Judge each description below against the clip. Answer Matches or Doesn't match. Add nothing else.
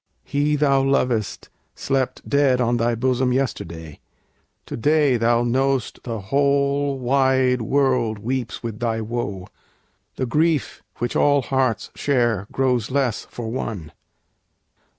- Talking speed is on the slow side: Matches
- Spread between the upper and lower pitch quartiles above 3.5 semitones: Doesn't match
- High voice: Doesn't match